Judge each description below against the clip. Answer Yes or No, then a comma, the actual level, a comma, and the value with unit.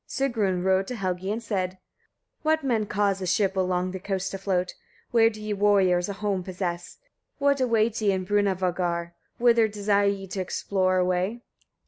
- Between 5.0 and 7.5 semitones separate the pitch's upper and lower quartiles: No, narrow, 2.6 semitones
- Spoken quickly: No, average, 180 wpm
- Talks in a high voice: Yes, high, 195 Hz